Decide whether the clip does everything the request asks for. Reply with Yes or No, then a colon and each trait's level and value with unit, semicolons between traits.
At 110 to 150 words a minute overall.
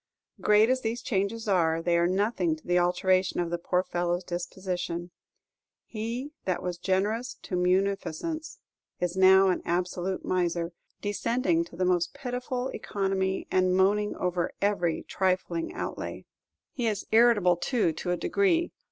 Yes: average, 145 wpm